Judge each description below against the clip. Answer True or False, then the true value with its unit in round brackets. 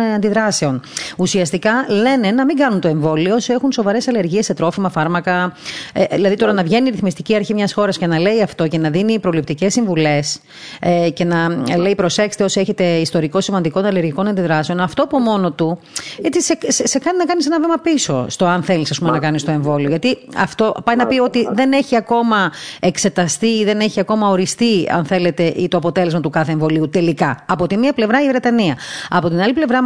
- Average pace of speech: False (200 wpm)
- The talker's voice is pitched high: True (195 Hz)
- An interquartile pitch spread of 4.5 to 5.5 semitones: True (5.1 semitones)